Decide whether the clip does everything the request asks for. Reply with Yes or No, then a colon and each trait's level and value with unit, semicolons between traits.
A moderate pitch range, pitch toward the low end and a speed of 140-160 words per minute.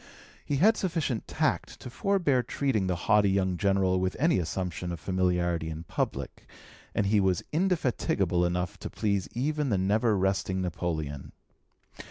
No: wide, 5.8 semitones; very low, 95 Hz; average, 150 wpm